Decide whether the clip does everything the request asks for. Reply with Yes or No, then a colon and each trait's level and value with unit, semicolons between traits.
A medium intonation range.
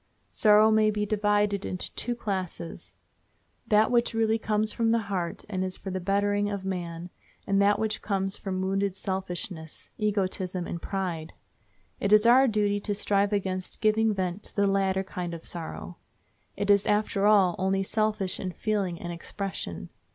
No: narrow, 2.2 semitones